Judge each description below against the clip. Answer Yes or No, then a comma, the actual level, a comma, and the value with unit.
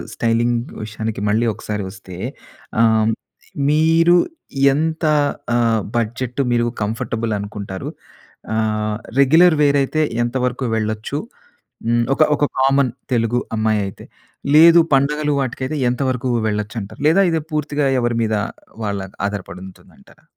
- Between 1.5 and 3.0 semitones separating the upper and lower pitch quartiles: No, average, 4.7 semitones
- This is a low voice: Yes, low, 120 Hz